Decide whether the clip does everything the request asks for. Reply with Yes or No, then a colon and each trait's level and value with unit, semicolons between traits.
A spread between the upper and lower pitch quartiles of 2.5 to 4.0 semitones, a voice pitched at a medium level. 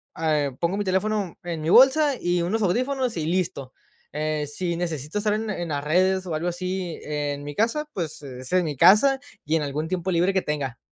No: average, 4.4 semitones; medium, 175 Hz